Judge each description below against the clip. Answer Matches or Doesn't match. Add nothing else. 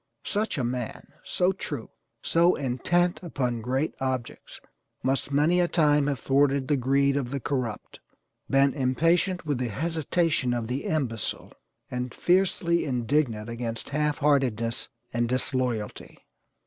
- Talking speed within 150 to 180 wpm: Doesn't match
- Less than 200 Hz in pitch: Matches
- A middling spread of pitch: Matches